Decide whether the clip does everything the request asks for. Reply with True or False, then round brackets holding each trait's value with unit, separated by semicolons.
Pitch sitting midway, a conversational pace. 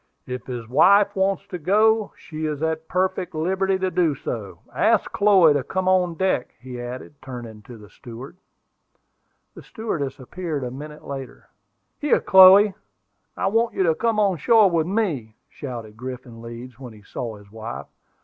True (155 Hz; 170 wpm)